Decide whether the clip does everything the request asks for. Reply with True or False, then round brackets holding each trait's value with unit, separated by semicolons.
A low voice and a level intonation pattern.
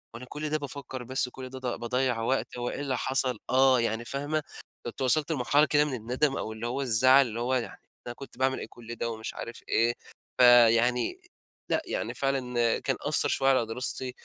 True (130 Hz; 2.3 semitones)